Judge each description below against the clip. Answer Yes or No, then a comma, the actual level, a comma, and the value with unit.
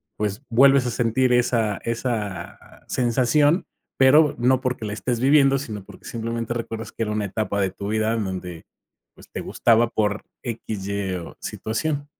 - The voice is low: Yes, low, 115 Hz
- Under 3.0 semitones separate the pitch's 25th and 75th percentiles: No, average, 3.5 semitones